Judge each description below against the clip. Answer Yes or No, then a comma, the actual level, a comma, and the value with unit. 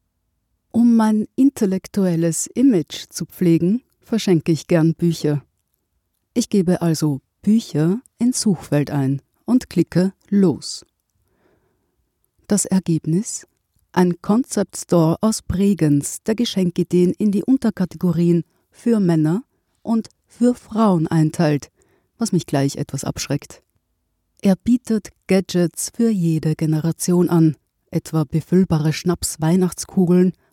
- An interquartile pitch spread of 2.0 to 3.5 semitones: No, average, 4.5 semitones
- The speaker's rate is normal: No, slow, 105 wpm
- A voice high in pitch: No, medium, 175 Hz